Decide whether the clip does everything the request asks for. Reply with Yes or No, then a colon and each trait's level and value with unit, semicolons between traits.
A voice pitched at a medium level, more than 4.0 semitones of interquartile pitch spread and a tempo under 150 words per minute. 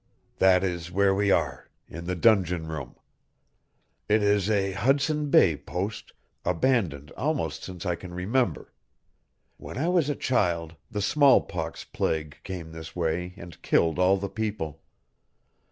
No: very low, 95 Hz; average, 4.4 semitones; average, 140 wpm